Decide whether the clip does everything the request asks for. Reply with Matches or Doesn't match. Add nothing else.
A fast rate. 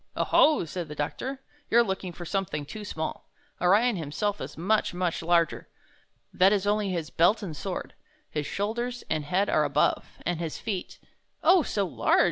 Doesn't match